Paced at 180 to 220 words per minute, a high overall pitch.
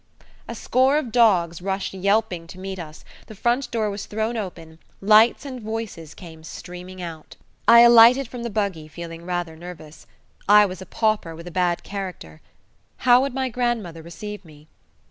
No: average, 170 wpm; high, 195 Hz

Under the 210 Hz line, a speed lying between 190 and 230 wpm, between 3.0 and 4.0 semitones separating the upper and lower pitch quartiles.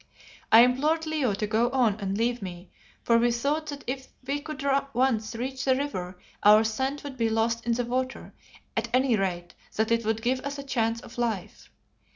No: high, 240 Hz; average, 195 wpm; average, 3.3 semitones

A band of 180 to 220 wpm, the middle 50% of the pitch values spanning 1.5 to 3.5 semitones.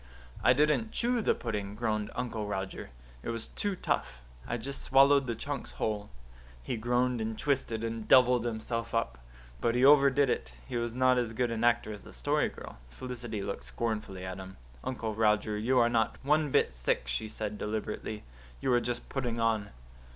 Yes: average, 185 wpm; average, 3.0 semitones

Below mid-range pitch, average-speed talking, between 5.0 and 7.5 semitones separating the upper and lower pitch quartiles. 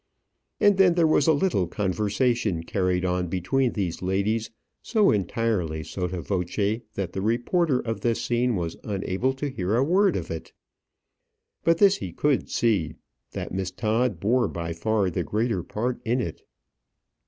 Yes: low, 105 Hz; average, 160 wpm; wide, 5.5 semitones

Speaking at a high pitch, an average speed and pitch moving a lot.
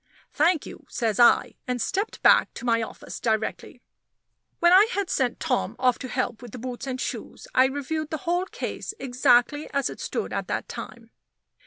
No: very high, 260 Hz; average, 185 wpm; average, 4.4 semitones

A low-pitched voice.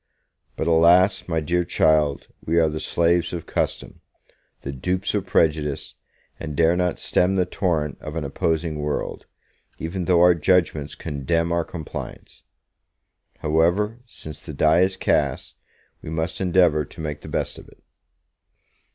Yes: very low, 80 Hz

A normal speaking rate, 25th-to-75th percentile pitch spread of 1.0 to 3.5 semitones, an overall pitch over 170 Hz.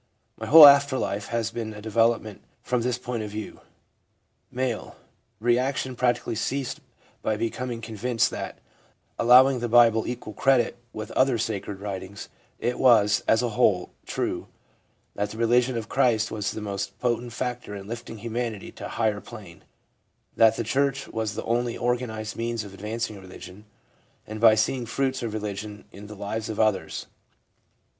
No: average, 170 wpm; narrow, 2.5 semitones; low, 115 Hz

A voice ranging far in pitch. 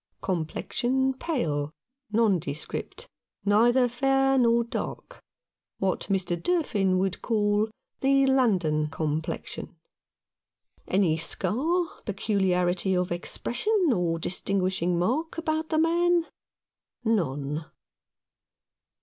Yes: wide, 7.1 semitones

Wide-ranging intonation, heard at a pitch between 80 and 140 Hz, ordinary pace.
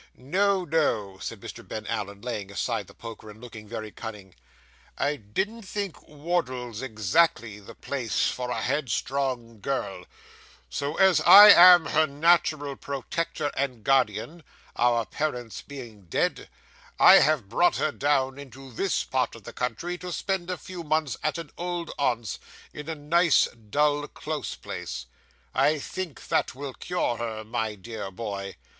Yes: wide, 6.2 semitones; low, 135 Hz; average, 150 wpm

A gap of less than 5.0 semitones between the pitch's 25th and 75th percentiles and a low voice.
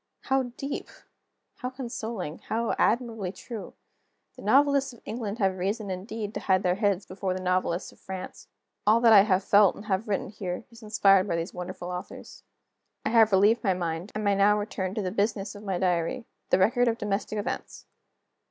No: average, 3.1 semitones; high, 205 Hz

